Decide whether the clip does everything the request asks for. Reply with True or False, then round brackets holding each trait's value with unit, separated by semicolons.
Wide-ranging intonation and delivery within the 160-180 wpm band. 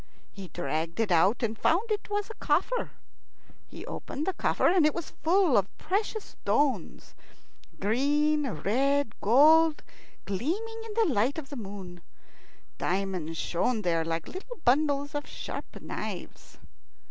False (9.0 semitones; 140 wpm)